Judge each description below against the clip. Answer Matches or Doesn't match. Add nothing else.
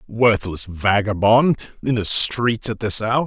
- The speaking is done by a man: Matches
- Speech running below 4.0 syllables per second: Matches